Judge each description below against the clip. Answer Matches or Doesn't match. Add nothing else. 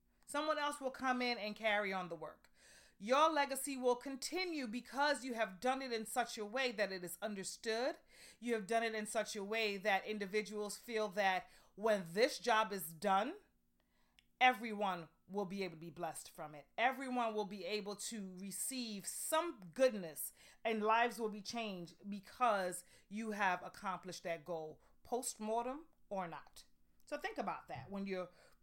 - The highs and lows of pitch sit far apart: Doesn't match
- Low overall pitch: Doesn't match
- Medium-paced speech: Matches